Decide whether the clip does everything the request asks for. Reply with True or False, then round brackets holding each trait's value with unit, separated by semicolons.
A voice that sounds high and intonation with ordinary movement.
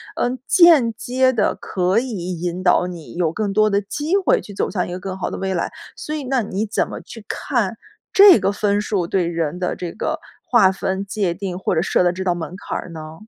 True (195 Hz; 4.3 semitones)